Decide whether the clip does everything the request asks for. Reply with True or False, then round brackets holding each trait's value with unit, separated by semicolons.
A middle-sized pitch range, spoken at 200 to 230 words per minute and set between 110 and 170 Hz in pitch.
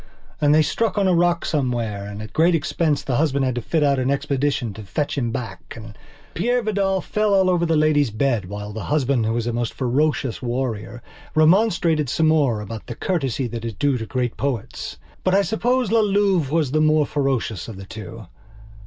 False (5.9 semitones; 205 wpm; 140 Hz)